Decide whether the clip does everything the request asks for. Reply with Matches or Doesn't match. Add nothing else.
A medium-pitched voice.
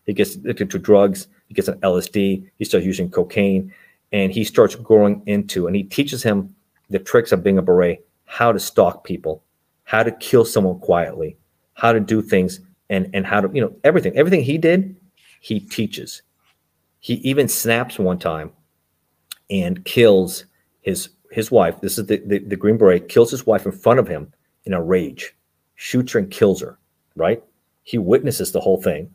Doesn't match